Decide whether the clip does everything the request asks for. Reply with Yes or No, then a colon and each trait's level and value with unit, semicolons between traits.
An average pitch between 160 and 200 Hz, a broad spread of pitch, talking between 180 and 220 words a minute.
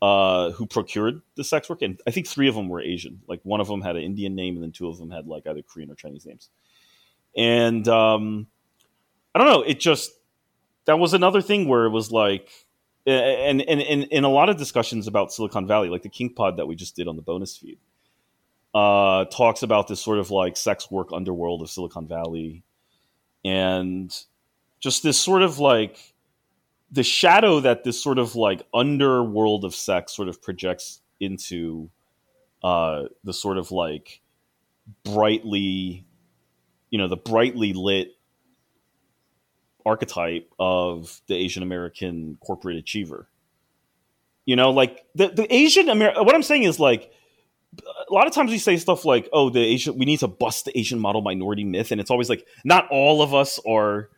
No: low, 105 Hz; wide, 6.2 semitones; average, 185 wpm